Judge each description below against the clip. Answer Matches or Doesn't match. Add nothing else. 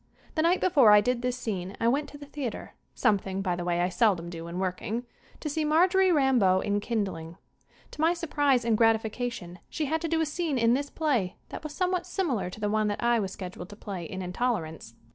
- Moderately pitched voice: Doesn't match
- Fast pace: Matches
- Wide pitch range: Matches